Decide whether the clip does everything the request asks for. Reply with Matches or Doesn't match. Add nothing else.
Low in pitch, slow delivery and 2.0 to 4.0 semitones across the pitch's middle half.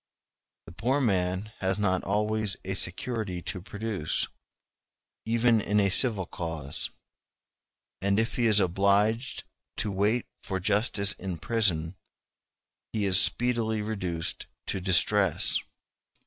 Matches